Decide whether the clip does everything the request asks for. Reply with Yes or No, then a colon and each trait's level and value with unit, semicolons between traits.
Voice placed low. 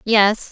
No: high, 210 Hz